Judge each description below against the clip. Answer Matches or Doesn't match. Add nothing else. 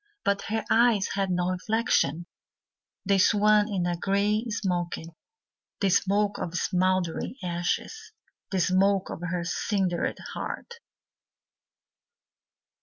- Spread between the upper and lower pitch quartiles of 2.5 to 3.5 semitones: Matches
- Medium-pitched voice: Doesn't match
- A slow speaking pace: Matches